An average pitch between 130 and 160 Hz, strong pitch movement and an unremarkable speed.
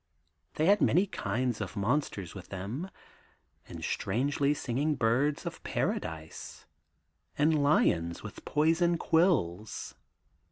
No: medium, 140 Hz; wide, 7.7 semitones; slow, 110 wpm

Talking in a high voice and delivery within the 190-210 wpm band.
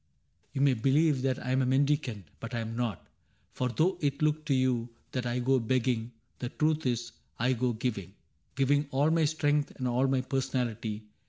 No: low, 130 Hz; average, 195 wpm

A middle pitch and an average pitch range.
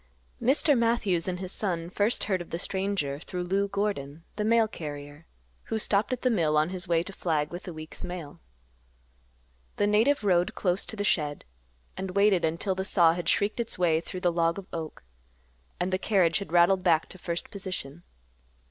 Yes: medium, 180 Hz; average, 3.4 semitones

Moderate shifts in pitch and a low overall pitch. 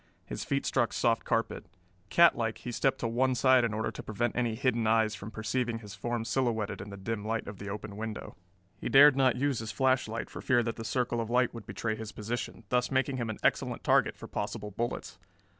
No: narrow, 2.3 semitones; low, 115 Hz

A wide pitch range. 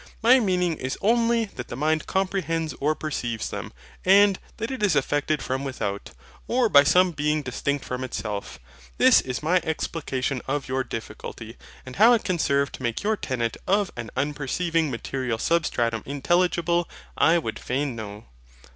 Yes: wide, 5.8 semitones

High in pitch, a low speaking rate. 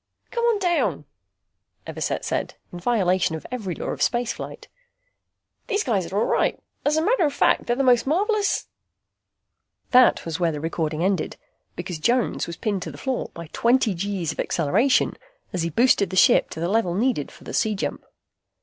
No: high, 205 Hz; average, 185 wpm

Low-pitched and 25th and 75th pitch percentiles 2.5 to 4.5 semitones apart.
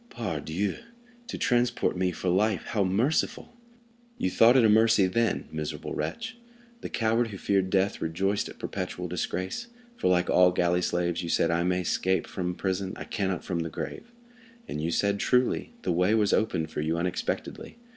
Yes: very low, 95 Hz; average, 3.7 semitones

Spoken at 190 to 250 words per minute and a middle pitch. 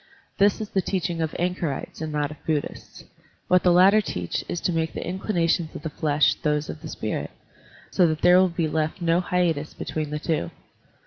Yes: average, 200 wpm; medium, 165 Hz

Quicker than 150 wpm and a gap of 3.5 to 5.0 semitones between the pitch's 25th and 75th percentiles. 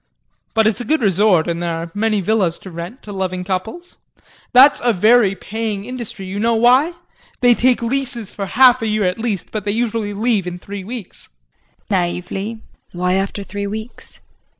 Yes: average, 185 wpm; average, 3.9 semitones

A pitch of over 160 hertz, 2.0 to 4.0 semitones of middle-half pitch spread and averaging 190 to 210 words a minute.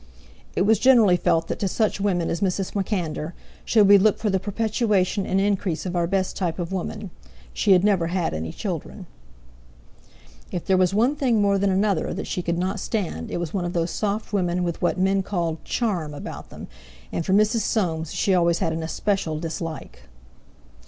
Yes: medium, 185 Hz; average, 3.1 semitones; average, 195 wpm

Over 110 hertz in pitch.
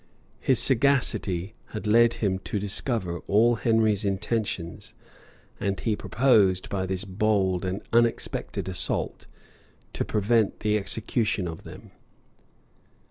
No: low, 105 Hz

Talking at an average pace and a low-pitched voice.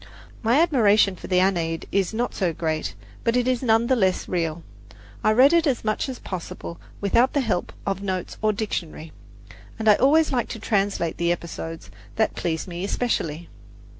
No: average, 180 wpm; high, 200 Hz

